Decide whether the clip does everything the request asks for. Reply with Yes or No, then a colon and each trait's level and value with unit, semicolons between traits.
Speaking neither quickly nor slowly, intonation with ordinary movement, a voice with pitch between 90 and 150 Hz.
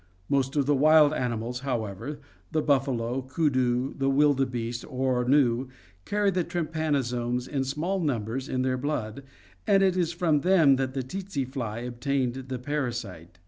Yes: average, 150 wpm; average, 3.3 semitones; low, 135 Hz